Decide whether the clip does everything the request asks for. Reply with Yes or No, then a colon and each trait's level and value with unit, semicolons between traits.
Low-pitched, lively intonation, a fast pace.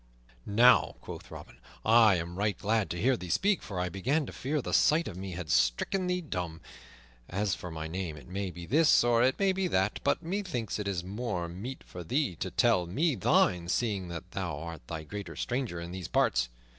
Yes: low, 100 Hz; wide, 6.5 semitones; fast, 210 wpm